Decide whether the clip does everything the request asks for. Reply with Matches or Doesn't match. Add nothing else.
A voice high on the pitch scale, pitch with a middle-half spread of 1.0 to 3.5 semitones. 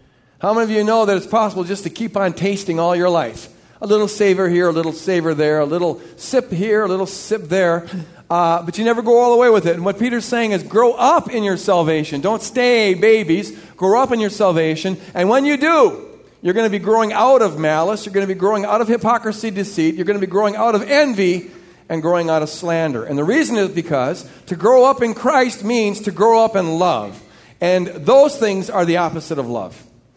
Doesn't match